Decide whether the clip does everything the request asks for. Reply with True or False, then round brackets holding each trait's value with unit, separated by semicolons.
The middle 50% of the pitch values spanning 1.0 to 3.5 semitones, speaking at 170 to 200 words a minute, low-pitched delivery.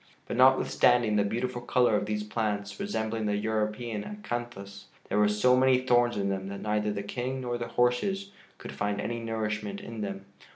True (2.9 semitones; 180 wpm; 110 Hz)